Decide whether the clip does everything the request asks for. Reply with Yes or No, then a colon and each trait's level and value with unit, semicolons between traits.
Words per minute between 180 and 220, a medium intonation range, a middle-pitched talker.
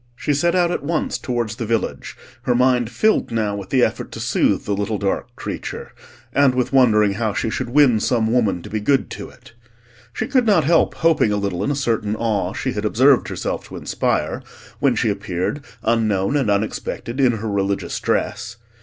No: average, 200 wpm; average, 4.5 semitones; low, 115 Hz